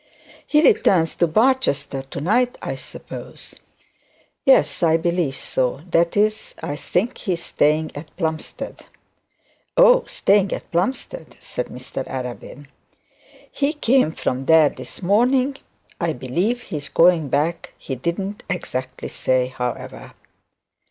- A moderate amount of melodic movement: No, wide, 7.3 semitones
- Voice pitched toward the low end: No, medium, 170 Hz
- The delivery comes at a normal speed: No, slow, 130 wpm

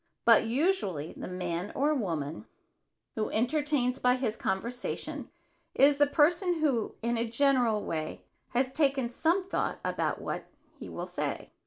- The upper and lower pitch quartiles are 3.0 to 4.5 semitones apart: No, average, 5.1 semitones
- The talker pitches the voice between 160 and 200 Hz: No, very high, 250 Hz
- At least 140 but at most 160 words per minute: Yes, average, 145 wpm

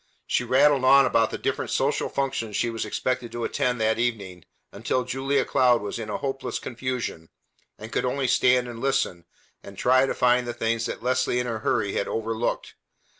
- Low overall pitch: Yes, low, 120 Hz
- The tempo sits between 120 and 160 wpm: No, average, 185 wpm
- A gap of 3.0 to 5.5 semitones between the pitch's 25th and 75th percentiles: No, narrow, 2.4 semitones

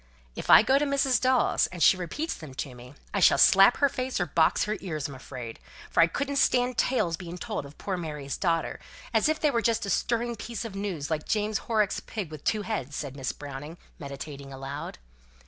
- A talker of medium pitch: Yes, medium, 180 Hz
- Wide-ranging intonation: Yes, wide, 8.0 semitones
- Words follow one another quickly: Yes, fast, 215 wpm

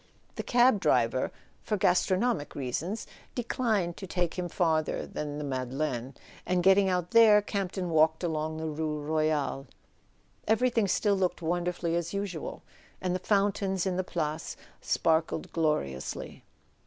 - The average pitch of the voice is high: No, medium, 175 Hz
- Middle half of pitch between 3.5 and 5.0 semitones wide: Yes, average, 4.1 semitones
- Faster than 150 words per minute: No, slow, 135 wpm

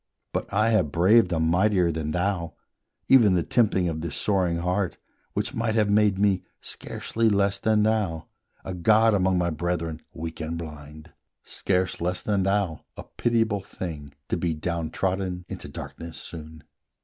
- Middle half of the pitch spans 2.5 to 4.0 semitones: Yes, average, 3.7 semitones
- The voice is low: Yes, very low, 90 Hz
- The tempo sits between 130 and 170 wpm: Yes, average, 160 wpm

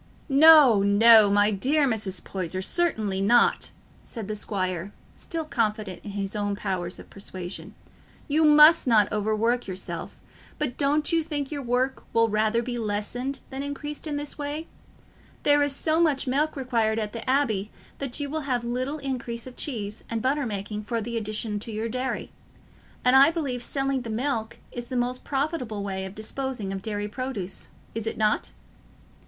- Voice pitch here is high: Yes, high, 235 Hz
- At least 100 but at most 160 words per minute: No, average, 170 wpm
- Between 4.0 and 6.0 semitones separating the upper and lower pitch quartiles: Yes, average, 4.9 semitones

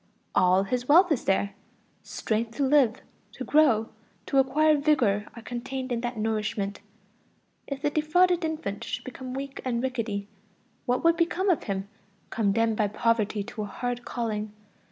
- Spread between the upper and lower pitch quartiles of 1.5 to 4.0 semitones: No, average, 5.1 semitones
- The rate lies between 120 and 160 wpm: Yes, average, 155 wpm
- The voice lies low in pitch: No, high, 240 Hz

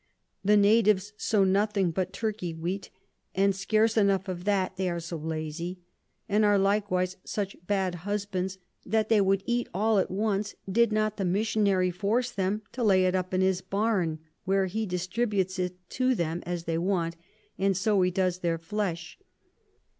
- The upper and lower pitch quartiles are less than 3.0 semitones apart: Yes, narrow, 2.4 semitones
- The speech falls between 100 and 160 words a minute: No, average, 170 wpm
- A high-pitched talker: Yes, high, 195 Hz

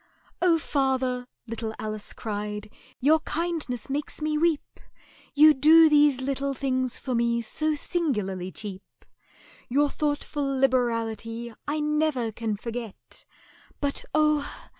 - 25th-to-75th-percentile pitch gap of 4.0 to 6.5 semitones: Yes, average, 4.7 semitones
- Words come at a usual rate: No, slow, 120 wpm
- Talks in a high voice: Yes, very high, 265 Hz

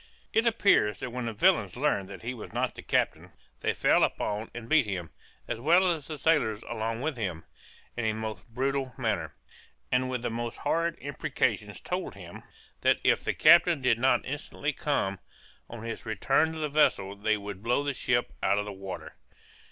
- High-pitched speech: No, low, 120 Hz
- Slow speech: No, average, 190 wpm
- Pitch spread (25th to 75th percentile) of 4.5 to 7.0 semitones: Yes, average, 5.0 semitones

